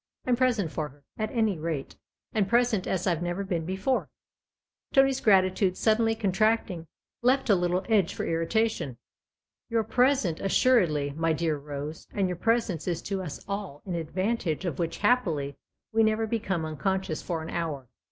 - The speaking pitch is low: No, high, 190 Hz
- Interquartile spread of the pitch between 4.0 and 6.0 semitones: Yes, average, 5.2 semitones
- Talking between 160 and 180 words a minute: Yes, average, 170 wpm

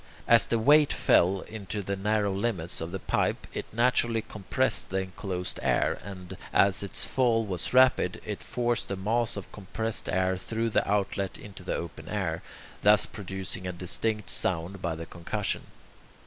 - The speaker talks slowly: No, average, 165 wpm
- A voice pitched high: No, low, 100 Hz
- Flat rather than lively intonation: No, average, 3.3 semitones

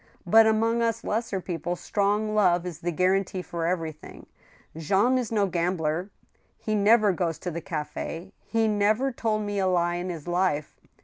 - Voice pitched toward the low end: No, high, 190 Hz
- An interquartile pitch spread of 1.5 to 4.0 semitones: Yes, average, 3.7 semitones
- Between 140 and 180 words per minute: Yes, average, 170 wpm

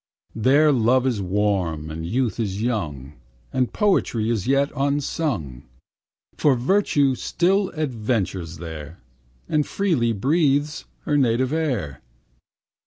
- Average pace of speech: No, slow, 110 wpm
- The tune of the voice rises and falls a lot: Yes, wide, 7.4 semitones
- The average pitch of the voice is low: Yes, low, 120 Hz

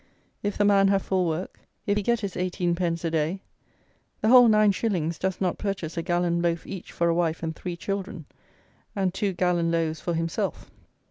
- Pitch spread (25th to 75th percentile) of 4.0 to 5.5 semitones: No, average, 2.8 semitones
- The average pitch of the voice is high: No, medium, 180 Hz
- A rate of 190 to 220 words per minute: Yes, average, 200 wpm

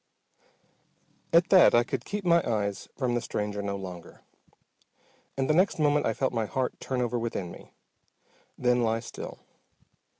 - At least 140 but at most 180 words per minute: Yes, average, 160 wpm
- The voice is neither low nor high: No, low, 120 Hz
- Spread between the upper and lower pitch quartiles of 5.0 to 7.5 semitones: Yes, average, 5.3 semitones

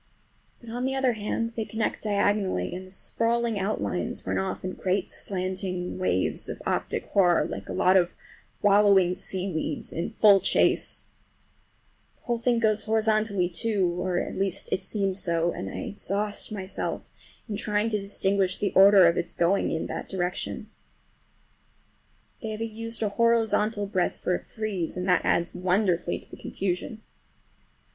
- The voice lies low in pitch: No, high, 200 Hz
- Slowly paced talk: No, average, 155 wpm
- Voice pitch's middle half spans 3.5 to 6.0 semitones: No, average, 3.0 semitones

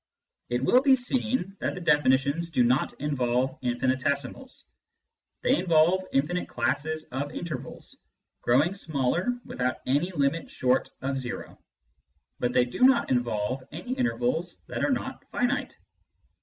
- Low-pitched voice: No, medium, 145 Hz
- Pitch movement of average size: No, wide, 6.5 semitones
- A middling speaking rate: No, slow, 130 wpm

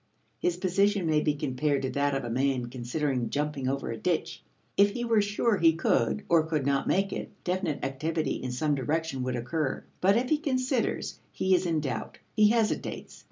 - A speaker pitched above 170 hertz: No, medium, 155 Hz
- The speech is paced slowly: No, average, 195 wpm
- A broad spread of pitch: Yes, wide, 6.2 semitones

